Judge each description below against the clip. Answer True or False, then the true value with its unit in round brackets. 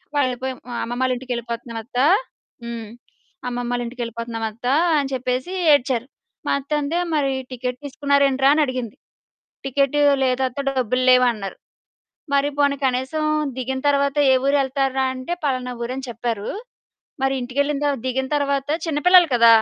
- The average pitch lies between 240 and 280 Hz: True (260 Hz)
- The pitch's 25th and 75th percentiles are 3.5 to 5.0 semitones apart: False (2.4 semitones)